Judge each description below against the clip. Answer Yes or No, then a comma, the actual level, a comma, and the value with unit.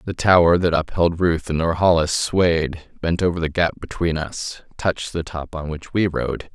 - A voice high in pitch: No, very low, 85 Hz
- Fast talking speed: No, average, 190 wpm